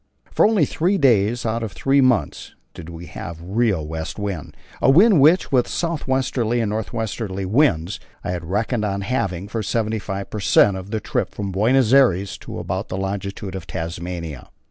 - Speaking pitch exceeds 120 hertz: No, low, 105 Hz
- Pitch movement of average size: Yes, average, 4.9 semitones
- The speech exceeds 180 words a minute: Yes, average, 190 wpm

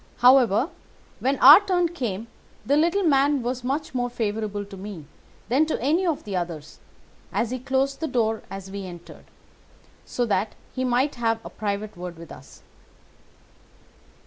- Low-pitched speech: No, high, 240 Hz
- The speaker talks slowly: No, average, 160 wpm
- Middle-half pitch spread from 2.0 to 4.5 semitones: No, wide, 5.4 semitones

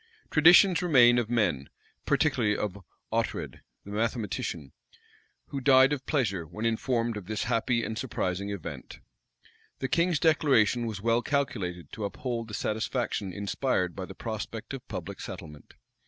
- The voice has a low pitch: Yes, low, 115 Hz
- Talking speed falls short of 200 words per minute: Yes, average, 140 wpm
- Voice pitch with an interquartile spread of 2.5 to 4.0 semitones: No, average, 4.6 semitones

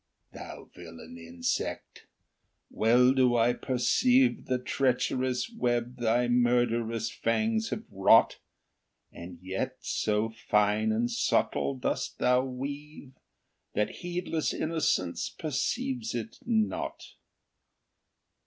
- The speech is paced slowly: Yes, slow, 95 wpm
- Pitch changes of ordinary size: No, wide, 5.9 semitones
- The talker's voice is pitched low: Yes, low, 125 Hz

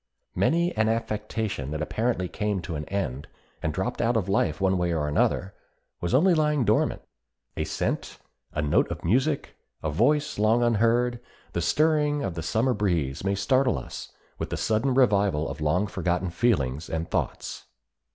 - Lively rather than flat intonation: Yes, wide, 6.4 semitones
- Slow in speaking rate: No, average, 170 wpm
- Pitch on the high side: No, low, 100 Hz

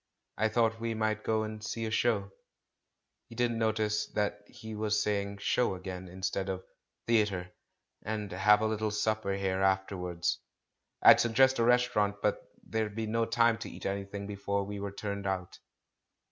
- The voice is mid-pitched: No, low, 105 Hz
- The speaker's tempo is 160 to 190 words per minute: Yes, average, 175 wpm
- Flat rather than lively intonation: Yes, narrow, 2.0 semitones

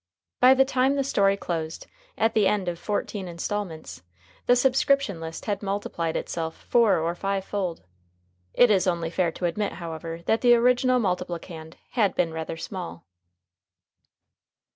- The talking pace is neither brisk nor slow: Yes, average, 150 wpm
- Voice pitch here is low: No, high, 190 Hz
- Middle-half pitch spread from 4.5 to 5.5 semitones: Yes, average, 5.1 semitones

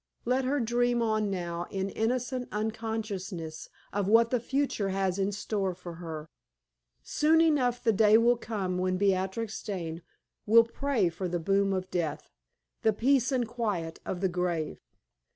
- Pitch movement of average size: Yes, average, 4.3 semitones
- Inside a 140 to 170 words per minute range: Yes, average, 155 wpm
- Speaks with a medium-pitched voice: No, high, 205 Hz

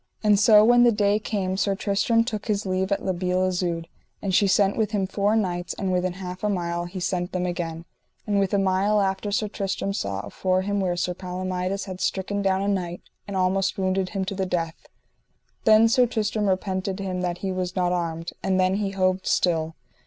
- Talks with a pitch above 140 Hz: Yes, high, 190 Hz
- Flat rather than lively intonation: Yes, narrow, 1.9 semitones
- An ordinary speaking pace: No, fast, 210 wpm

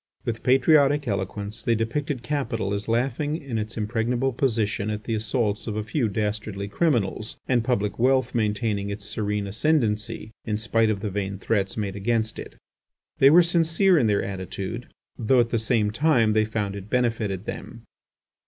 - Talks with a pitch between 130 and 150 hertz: No, low, 110 Hz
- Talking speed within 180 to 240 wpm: No, average, 170 wpm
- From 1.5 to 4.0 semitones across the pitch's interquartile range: Yes, average, 3.3 semitones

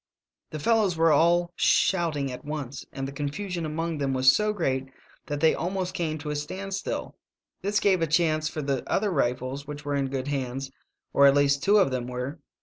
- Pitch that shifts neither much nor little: Yes, average, 4.1 semitones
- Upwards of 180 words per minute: Yes, fast, 205 wpm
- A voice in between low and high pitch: Yes, medium, 150 Hz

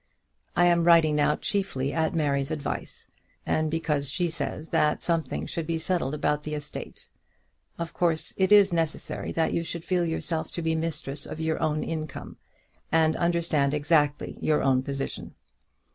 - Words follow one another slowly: No, average, 165 wpm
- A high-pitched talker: No, medium, 160 Hz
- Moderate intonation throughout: No, narrow, 2.1 semitones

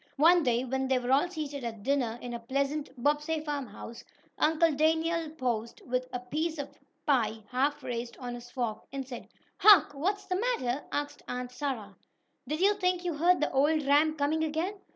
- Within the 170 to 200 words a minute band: Yes, average, 185 wpm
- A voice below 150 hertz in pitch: No, very high, 285 Hz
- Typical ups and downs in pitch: Yes, average, 4.2 semitones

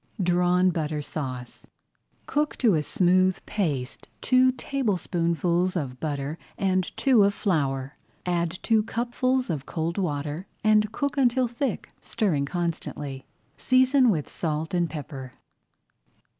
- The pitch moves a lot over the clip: Yes, wide, 6.6 semitones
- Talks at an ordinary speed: No, slow, 120 wpm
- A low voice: No, medium, 180 Hz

